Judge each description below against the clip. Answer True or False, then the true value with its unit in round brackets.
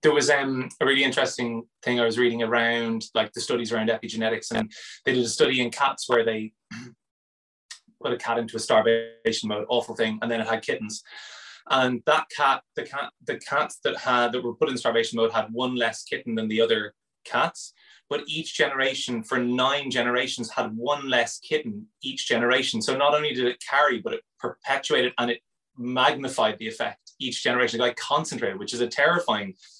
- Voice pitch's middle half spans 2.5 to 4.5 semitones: True (2.8 semitones)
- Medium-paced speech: True (195 wpm)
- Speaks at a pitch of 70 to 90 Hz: False (120 Hz)